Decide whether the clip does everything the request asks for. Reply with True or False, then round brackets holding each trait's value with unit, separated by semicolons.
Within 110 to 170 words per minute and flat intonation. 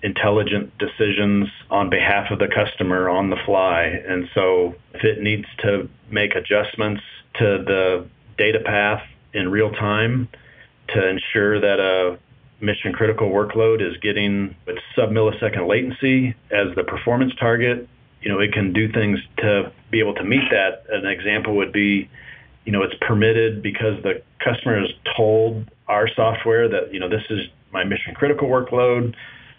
True (155 wpm; 2.1 semitones)